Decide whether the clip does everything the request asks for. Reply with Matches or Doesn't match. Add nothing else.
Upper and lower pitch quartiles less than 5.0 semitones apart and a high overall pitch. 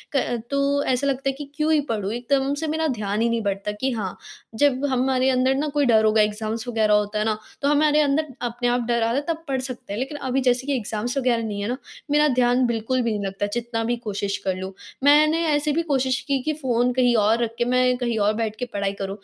Matches